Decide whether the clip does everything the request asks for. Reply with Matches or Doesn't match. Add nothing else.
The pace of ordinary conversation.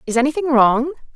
Matches